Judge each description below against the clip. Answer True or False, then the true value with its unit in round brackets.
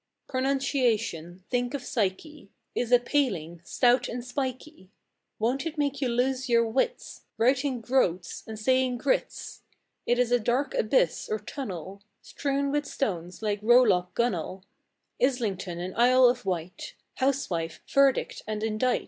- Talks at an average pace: False (130 wpm)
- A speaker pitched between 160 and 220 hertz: False (245 Hz)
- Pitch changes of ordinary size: True (5.0 semitones)